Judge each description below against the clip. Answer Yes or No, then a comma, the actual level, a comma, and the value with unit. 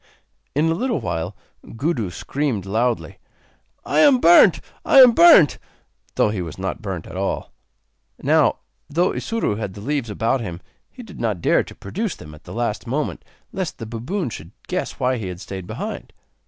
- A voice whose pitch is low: Yes, low, 115 Hz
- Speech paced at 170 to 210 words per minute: Yes, average, 180 wpm